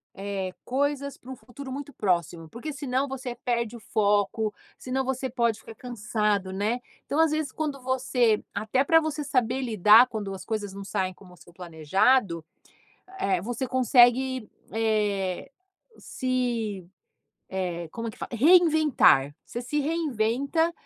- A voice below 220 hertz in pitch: No, high, 235 Hz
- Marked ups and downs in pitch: No, average, 4.7 semitones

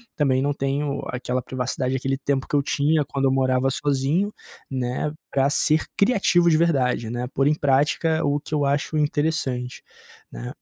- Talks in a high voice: No, medium, 140 Hz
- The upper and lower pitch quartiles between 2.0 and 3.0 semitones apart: Yes, narrow, 2.4 semitones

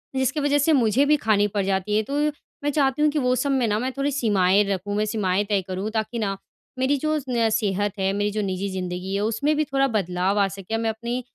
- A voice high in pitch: Yes, high, 215 Hz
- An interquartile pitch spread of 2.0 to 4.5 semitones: No, average, 5.0 semitones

